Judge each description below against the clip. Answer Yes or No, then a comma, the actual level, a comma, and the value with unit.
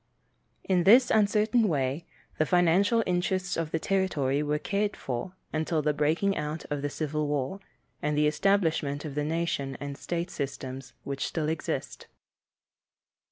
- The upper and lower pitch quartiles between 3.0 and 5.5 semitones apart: Yes, average, 4.3 semitones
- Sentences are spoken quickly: No, average, 150 wpm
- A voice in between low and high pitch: Yes, medium, 155 Hz